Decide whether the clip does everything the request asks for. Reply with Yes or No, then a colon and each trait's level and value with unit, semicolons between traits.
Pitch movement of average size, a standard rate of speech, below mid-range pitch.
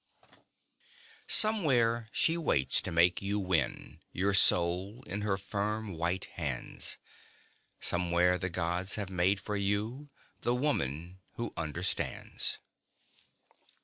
No: average, 3.7 semitones; slow, 110 wpm; very low, 95 Hz